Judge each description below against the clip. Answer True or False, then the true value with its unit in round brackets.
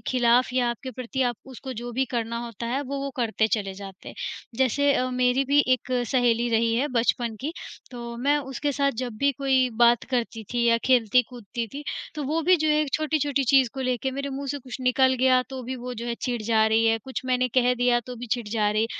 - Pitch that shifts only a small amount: True (2.2 semitones)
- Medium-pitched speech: False (250 Hz)